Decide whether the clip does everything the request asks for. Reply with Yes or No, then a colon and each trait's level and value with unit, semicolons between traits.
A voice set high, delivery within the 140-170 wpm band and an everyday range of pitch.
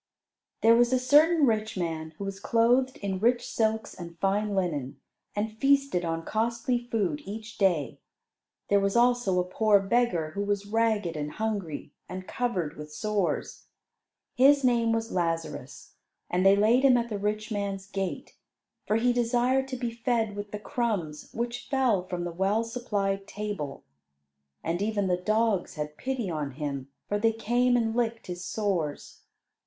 Yes: high, 210 Hz; average, 165 wpm; average, 4.5 semitones